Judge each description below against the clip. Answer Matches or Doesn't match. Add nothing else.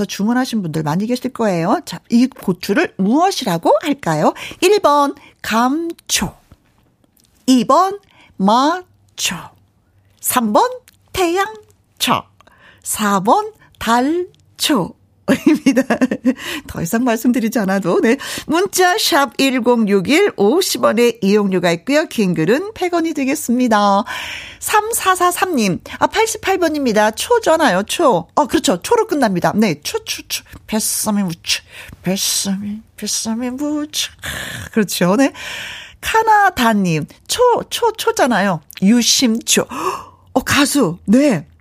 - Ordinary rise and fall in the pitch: Doesn't match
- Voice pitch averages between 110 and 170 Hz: Doesn't match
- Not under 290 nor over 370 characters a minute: Doesn't match